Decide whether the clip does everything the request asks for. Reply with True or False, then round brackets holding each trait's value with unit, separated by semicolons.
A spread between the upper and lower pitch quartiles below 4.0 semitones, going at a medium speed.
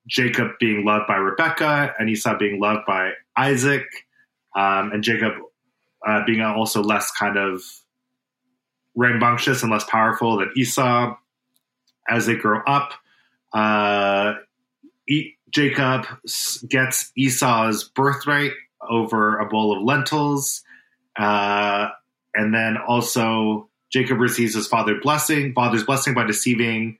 False (3.4 semitones; 120 wpm)